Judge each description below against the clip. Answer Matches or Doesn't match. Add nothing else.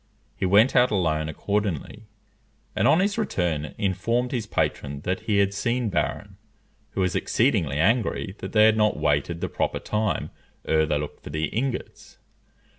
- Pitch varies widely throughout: Matches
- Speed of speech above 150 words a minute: Matches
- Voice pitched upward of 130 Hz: Doesn't match